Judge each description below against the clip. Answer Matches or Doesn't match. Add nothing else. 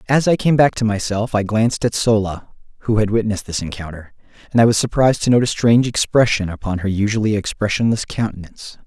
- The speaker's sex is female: Doesn't match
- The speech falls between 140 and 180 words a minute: Doesn't match